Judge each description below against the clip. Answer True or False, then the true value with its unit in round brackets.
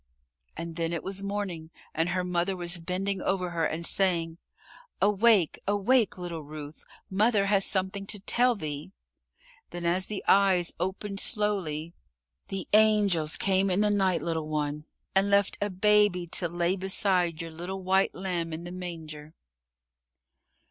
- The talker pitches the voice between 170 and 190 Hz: True (185 Hz)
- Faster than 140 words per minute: True (150 wpm)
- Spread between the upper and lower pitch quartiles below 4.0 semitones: True (3.0 semitones)